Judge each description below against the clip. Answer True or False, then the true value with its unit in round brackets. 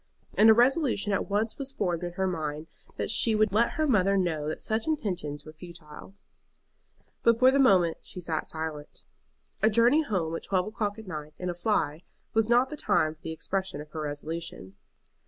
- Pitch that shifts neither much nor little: False (5.7 semitones)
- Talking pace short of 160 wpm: False (195 wpm)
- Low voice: False (190 Hz)